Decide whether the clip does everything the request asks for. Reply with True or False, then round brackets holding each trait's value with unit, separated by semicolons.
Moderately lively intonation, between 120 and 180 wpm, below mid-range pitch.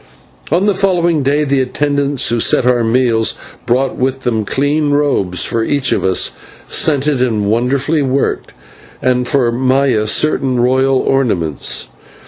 True (3.1 semitones; 140 wpm; 130 Hz)